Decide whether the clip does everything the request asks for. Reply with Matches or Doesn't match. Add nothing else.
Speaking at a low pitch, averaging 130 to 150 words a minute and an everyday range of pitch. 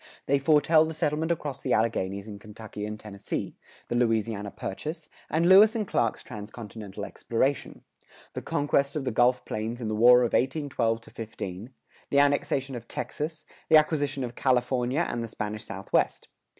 Doesn't match